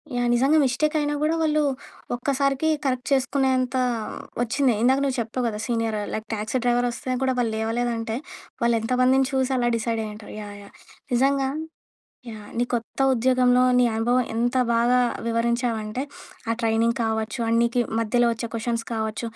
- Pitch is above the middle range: Yes, high, 245 Hz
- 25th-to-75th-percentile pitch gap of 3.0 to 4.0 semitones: No, narrow, 2.4 semitones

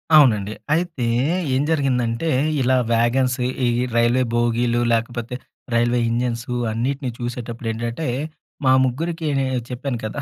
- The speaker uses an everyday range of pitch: No, narrow, 2.1 semitones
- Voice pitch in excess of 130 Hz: No, low, 120 Hz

